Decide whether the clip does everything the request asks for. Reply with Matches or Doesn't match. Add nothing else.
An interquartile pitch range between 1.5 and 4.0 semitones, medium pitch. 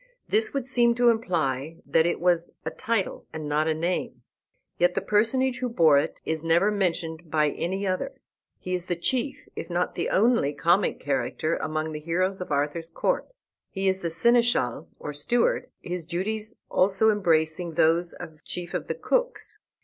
Doesn't match